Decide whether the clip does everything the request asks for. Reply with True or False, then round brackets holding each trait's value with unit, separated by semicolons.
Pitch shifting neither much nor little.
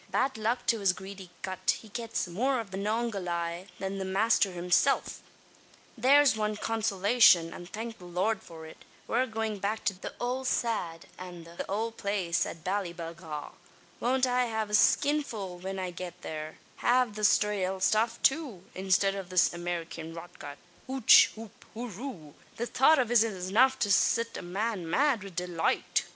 True (4.5 semitones)